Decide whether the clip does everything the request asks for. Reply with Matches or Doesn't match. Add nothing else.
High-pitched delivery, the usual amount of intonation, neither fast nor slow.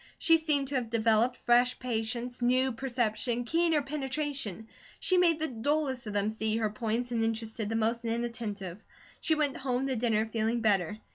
Matches